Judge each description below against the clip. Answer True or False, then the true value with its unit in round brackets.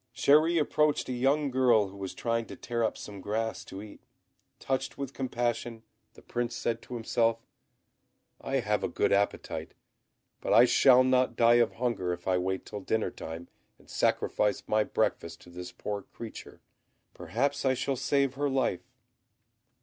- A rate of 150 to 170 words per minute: True (165 wpm)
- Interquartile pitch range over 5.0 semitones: False (4.1 semitones)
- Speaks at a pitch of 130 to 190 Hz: False (115 Hz)